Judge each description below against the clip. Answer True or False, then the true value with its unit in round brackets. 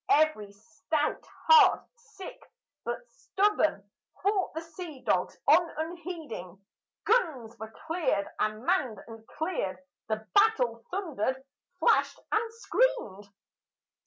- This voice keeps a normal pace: False (105 wpm)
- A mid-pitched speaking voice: False (315 Hz)